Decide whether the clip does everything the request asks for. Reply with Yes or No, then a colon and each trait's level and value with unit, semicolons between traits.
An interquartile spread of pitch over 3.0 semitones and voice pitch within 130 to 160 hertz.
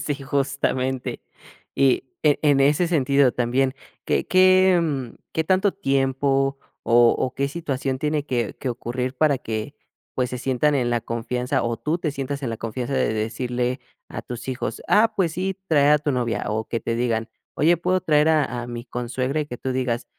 Yes: average, 3.5 semitones; low, 135 Hz